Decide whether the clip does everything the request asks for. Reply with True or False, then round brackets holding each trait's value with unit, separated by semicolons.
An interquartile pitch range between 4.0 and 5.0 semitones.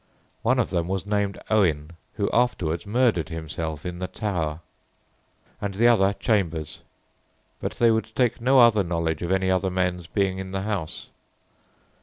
True (4.3 semitones)